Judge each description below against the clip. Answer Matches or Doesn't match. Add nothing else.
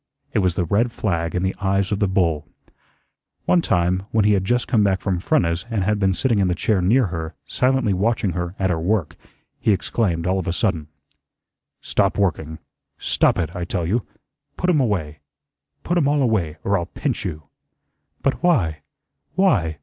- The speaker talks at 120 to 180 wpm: Doesn't match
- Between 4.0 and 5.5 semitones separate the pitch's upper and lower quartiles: Matches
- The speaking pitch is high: Doesn't match